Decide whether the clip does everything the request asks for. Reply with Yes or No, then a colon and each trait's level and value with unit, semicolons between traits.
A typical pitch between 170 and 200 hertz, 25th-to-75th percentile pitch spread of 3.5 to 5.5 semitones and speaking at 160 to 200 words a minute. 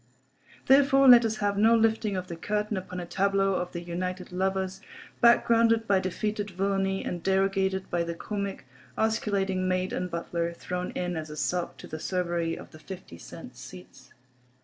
No: high, 190 Hz; average, 2.7 semitones; average, 170 wpm